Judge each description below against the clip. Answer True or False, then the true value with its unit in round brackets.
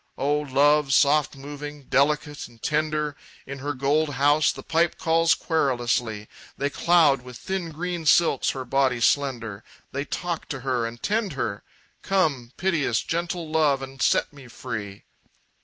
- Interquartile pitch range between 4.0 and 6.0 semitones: False (3.3 semitones)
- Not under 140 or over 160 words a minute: True (150 wpm)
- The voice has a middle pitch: True (145 Hz)